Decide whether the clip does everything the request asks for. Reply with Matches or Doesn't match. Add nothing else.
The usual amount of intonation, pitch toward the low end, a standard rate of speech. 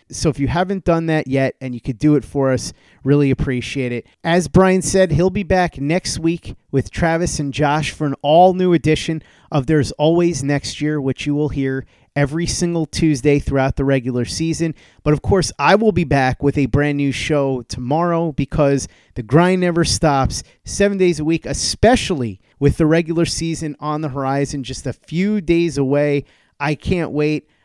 Doesn't match